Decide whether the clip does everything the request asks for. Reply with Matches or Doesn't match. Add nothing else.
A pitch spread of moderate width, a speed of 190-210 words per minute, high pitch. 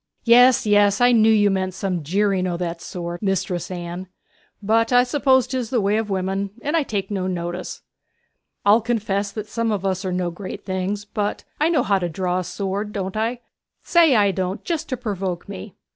Matches